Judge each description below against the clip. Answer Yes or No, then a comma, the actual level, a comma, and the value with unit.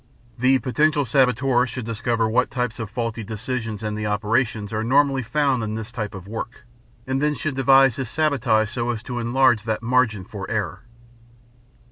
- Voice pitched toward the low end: Yes, low, 120 Hz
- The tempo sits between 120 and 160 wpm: No, average, 175 wpm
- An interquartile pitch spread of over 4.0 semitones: No, average, 3.1 semitones